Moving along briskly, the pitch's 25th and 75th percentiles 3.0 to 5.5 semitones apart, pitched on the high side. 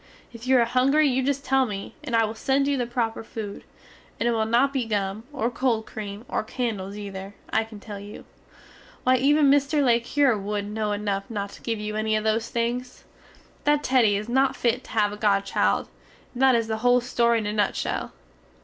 Yes: fast, 215 wpm; average, 3.4 semitones; high, 230 Hz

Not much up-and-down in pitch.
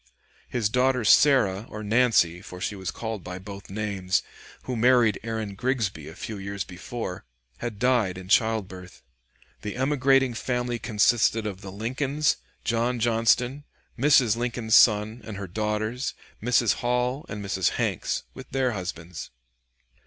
No: average, 3.8 semitones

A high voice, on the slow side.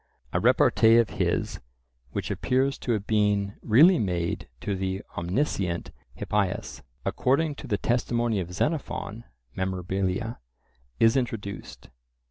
No: low, 105 Hz; slow, 115 wpm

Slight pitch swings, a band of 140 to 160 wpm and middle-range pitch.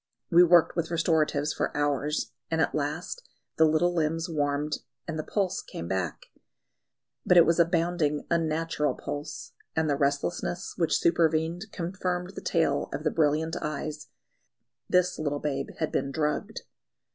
Yes: narrow, 2.3 semitones; average, 150 wpm; medium, 160 Hz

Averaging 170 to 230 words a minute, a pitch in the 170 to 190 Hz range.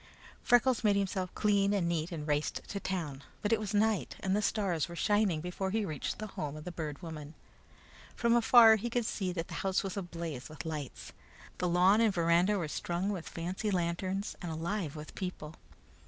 Yes: average, 200 wpm; medium, 185 Hz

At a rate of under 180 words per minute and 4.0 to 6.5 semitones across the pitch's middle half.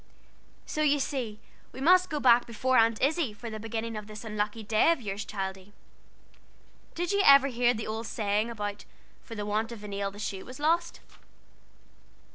No: average, 185 wpm; average, 4.4 semitones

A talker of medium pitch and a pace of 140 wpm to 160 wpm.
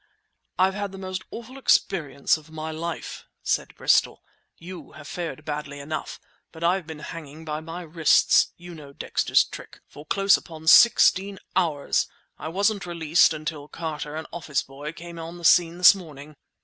Yes: medium, 165 Hz; average, 155 wpm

